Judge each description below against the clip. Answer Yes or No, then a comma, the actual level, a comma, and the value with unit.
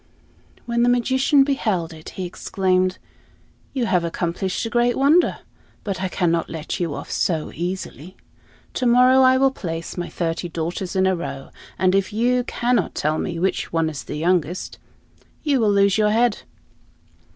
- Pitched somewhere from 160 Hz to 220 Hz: Yes, high, 190 Hz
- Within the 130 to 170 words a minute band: Yes, average, 165 wpm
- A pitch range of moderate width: No, wide, 6.1 semitones